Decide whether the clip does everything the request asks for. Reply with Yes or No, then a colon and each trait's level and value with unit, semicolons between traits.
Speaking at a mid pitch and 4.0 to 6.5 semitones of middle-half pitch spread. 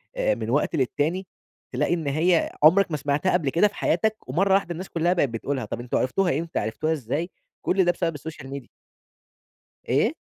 Yes: medium, 165 Hz; average, 4.6 semitones